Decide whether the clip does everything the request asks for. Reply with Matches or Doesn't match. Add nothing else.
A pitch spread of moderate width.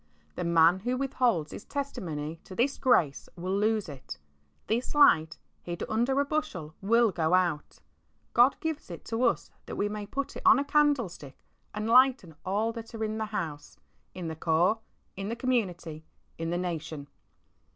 Doesn't match